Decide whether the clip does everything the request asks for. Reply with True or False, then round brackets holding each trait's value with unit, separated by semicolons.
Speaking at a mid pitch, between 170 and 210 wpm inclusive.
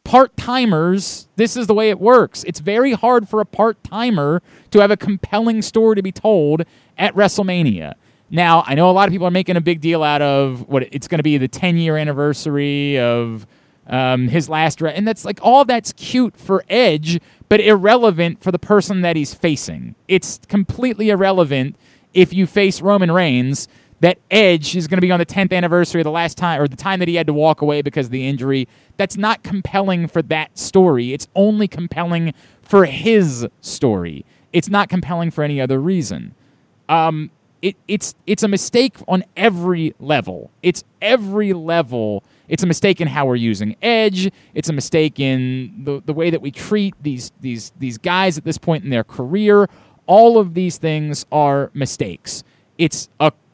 True (170 Hz; 190 wpm)